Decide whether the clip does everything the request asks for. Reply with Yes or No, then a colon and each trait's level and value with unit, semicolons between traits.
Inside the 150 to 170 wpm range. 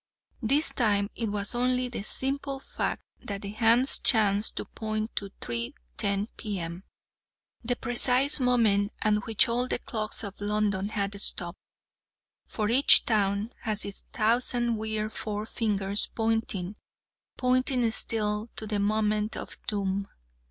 No: slow, 135 wpm